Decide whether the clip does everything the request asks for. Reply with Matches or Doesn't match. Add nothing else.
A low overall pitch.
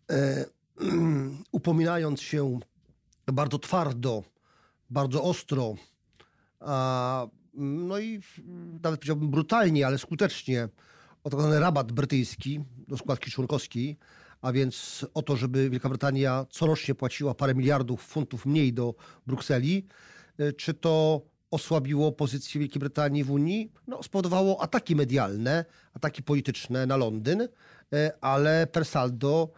Doesn't match